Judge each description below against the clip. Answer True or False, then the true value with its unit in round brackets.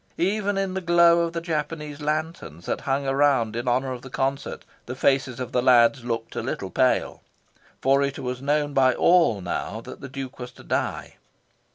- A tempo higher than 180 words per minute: True (195 wpm)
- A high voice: False (135 Hz)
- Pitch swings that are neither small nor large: True (4.0 semitones)